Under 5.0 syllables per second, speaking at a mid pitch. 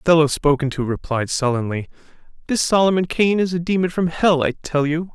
No: 5.7 syllables/s; medium, 160 Hz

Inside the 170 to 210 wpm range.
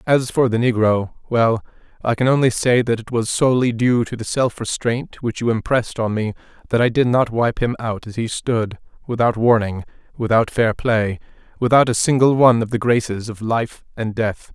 Yes: average, 190 wpm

